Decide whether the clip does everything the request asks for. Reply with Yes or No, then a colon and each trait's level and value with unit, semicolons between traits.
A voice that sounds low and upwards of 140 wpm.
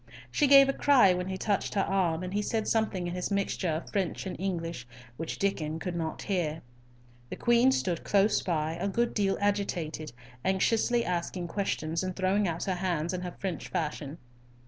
No: medium, 185 Hz; average, 190 wpm